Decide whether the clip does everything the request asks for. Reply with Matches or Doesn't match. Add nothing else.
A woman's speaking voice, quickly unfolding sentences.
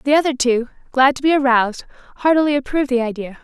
Doesn't match